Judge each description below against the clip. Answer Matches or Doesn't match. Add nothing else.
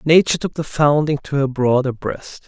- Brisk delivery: Doesn't match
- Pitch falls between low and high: Matches